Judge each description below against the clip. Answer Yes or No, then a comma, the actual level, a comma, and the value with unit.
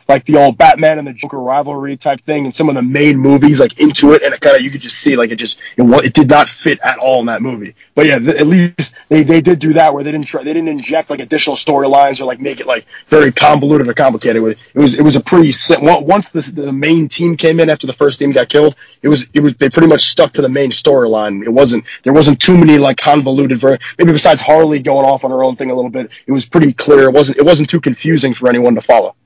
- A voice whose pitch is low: No, medium, 145 Hz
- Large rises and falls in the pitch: No, narrow, 2.5 semitones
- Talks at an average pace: No, fast, 280 wpm